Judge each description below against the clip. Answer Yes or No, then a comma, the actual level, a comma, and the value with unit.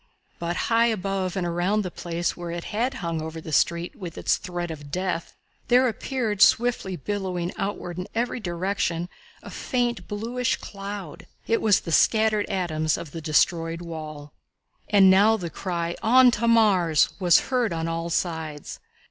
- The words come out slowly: No, average, 165 wpm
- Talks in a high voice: No, medium, 180 Hz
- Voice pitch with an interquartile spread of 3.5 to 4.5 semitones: Yes, average, 4.1 semitones